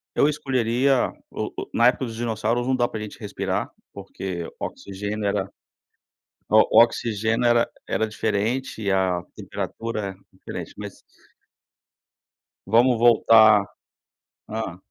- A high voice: No, low, 110 Hz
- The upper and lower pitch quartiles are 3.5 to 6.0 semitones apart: No, average, 2.9 semitones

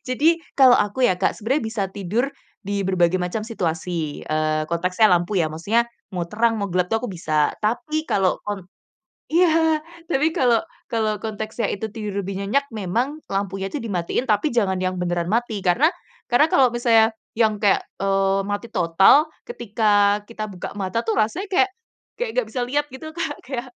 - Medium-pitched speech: No, high, 215 Hz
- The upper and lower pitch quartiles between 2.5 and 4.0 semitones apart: No, average, 4.6 semitones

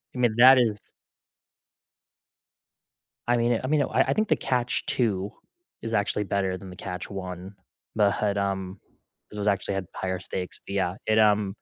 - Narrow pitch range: No, average, 3.6 semitones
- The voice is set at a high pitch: No, low, 100 Hz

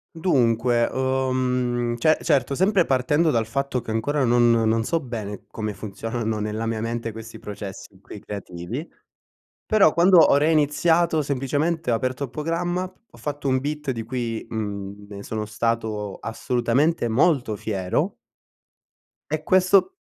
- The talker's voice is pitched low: Yes, low, 125 Hz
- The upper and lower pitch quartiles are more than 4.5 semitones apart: Yes, average, 5.1 semitones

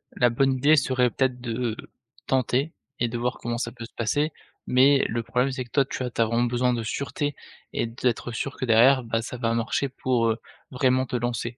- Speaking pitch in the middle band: No, low, 125 Hz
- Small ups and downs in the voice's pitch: Yes, narrow, 2.0 semitones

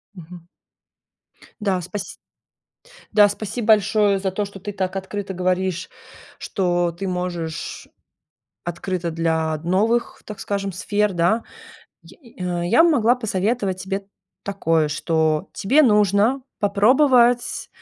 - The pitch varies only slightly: No, average, 3.1 semitones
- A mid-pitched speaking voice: No, high, 195 Hz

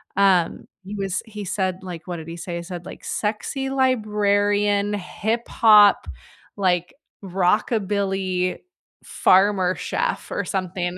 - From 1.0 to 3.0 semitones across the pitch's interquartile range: Yes, narrow, 2.4 semitones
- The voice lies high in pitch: Yes, high, 195 Hz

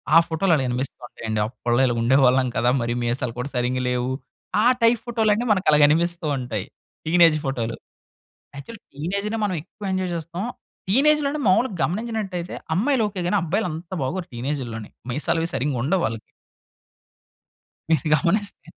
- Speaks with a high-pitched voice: No, medium, 165 Hz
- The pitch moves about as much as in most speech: No, wide, 7.8 semitones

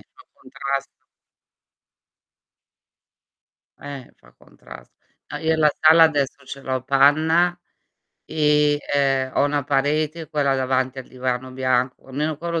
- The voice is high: No, medium, 140 Hz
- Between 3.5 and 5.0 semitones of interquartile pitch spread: No, average, 2.8 semitones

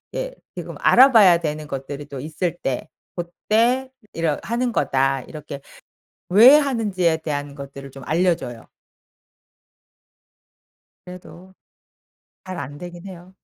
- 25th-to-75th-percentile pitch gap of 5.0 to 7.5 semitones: Yes, wide, 5.6 semitones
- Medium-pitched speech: Yes, medium, 170 Hz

